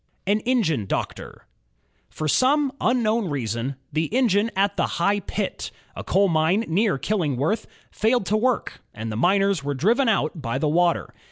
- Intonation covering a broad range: Yes, wide, 6.2 semitones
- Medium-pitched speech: No, high, 195 Hz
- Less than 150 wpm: No, average, 160 wpm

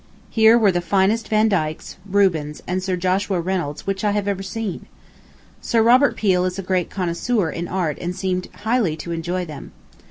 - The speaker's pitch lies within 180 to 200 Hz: Yes, medium, 185 Hz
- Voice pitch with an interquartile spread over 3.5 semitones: No, average, 2.9 semitones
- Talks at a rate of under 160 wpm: No, average, 170 wpm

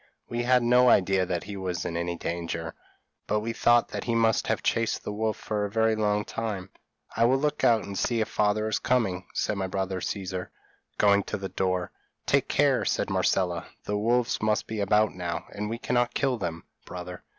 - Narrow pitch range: No, average, 3.7 semitones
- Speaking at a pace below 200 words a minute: No, fast, 205 wpm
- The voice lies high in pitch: No, low, 105 Hz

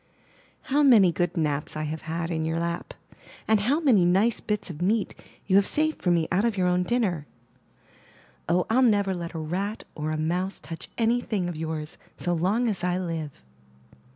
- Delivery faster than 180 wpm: Yes, average, 195 wpm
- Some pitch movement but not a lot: Yes, average, 4.5 semitones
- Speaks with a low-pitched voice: No, medium, 180 Hz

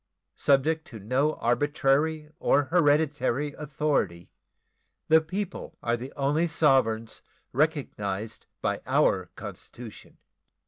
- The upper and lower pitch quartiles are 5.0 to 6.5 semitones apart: No, average, 4.5 semitones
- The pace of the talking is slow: Yes, slow, 95 wpm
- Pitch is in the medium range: Yes, medium, 145 Hz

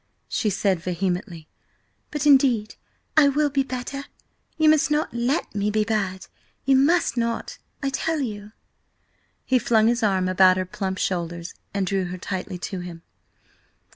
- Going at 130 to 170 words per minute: Yes, average, 150 wpm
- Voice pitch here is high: Yes, high, 210 Hz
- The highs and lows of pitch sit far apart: Yes, wide, 6.5 semitones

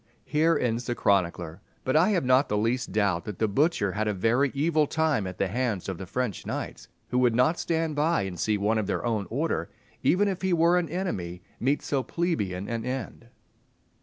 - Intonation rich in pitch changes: Yes, wide, 7.6 semitones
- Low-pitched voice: Yes, low, 120 Hz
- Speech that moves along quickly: Yes, fast, 210 wpm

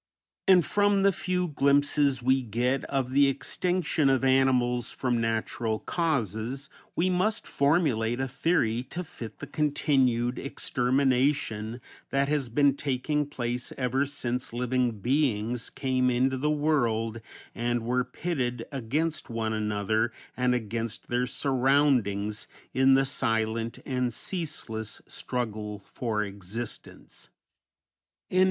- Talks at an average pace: No, slow, 120 wpm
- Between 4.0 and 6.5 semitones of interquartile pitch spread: No, average, 3.6 semitones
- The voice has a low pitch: Yes, low, 125 Hz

